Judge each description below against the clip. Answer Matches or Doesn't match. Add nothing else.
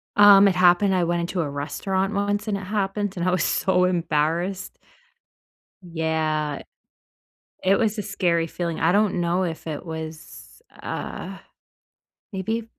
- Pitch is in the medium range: Matches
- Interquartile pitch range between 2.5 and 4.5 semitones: Matches